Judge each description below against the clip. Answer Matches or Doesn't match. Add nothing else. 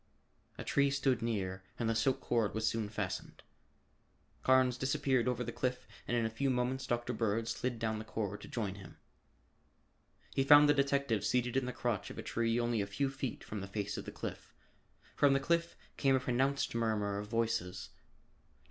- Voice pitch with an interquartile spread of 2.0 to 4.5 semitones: Matches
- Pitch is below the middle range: Matches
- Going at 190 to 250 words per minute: Matches